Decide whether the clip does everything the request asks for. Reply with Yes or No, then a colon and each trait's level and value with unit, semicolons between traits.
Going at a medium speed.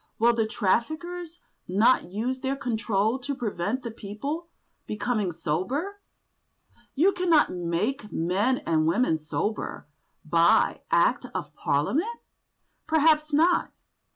No: slow, 110 wpm